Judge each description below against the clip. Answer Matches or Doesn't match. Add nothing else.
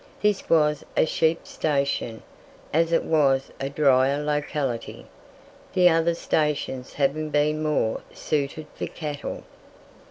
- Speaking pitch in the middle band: Matches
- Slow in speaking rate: Matches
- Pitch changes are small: Matches